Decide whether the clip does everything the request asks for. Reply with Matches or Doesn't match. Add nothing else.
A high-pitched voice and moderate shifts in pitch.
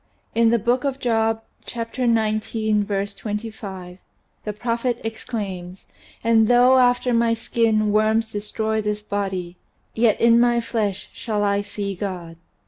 Doesn't match